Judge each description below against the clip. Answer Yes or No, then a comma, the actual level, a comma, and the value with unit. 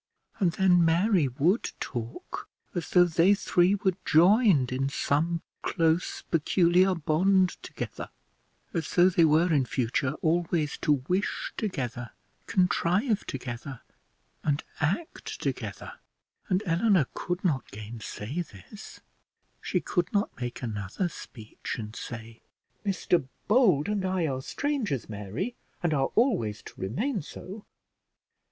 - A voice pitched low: No, medium, 165 Hz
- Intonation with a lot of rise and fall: Yes, wide, 6.1 semitones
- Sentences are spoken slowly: Yes, slow, 125 wpm